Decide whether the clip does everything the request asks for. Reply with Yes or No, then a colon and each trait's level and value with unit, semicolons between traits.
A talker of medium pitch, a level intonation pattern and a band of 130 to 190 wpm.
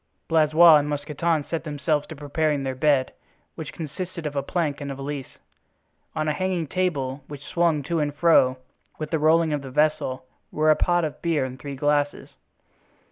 Yes: medium, 150 Hz; narrow, 2.3 semitones; average, 185 wpm